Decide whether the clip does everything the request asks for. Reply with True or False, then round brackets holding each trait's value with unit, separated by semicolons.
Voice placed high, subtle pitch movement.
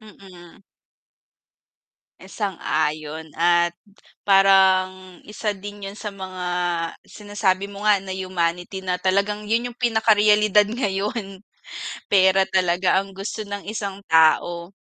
True (195 Hz; 2.0 semitones)